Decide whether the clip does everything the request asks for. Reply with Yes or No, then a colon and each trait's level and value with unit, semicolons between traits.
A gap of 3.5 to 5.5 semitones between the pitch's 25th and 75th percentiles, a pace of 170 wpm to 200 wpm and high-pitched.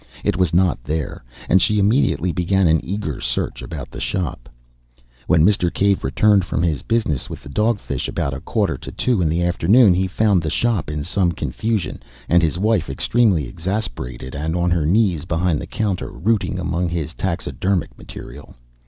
No: average, 4.1 semitones; average, 180 wpm; very low, 90 Hz